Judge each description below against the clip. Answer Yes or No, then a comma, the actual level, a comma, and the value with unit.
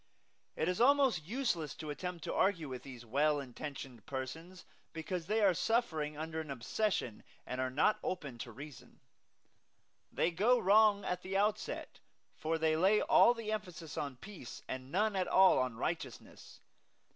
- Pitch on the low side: No, medium, 165 Hz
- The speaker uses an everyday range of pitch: No, wide, 6.3 semitones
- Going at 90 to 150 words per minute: No, average, 160 wpm